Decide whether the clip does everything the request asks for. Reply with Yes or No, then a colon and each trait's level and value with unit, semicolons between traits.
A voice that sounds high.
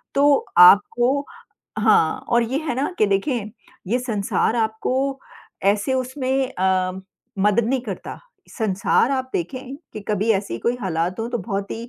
Yes: high, 225 Hz